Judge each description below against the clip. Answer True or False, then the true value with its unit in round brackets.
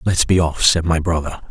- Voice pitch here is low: True (85 Hz)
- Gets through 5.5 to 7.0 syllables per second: True (6.0 syllables/s)